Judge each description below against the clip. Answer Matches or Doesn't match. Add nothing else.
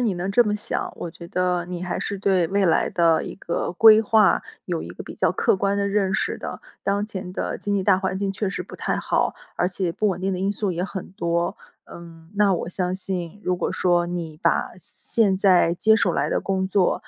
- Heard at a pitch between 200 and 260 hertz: Doesn't match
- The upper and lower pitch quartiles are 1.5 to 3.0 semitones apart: Matches